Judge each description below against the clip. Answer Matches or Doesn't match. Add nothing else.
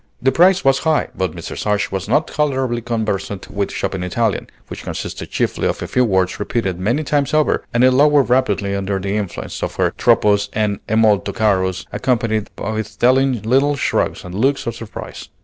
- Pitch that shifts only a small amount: Doesn't match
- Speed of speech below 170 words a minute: Doesn't match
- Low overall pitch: Matches